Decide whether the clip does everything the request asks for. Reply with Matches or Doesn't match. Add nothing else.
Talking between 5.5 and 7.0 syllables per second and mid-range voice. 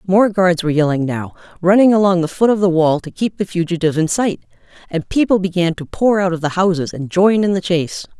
Matches